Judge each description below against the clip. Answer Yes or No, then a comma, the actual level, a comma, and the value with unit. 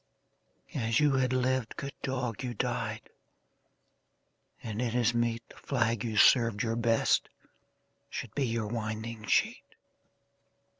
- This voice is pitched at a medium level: No, low, 115 Hz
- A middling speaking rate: No, slow, 130 wpm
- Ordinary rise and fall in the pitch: No, narrow, 1.9 semitones